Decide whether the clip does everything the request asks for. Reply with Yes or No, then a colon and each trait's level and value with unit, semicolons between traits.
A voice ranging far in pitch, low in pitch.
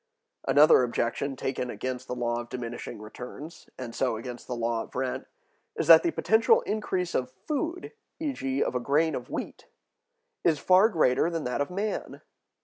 Yes: wide, 6.1 semitones; low, 130 Hz